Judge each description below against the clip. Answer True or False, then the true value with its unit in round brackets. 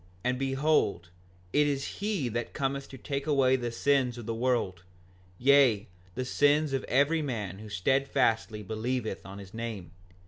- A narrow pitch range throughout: False (4.0 semitones)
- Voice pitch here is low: True (125 Hz)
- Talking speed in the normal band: True (160 wpm)